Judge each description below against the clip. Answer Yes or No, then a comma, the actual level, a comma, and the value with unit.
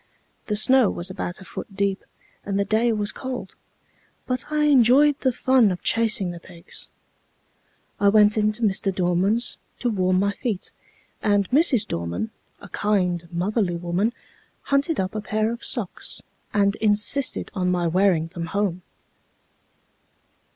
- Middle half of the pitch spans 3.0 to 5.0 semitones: Yes, average, 4.1 semitones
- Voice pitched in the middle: No, high, 205 Hz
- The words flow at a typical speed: Yes, average, 145 wpm